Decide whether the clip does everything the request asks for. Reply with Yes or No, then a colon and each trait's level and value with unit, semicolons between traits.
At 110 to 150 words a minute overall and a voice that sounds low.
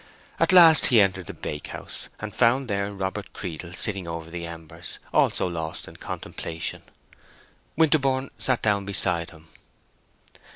Yes: slow, 135 wpm; low, 100 Hz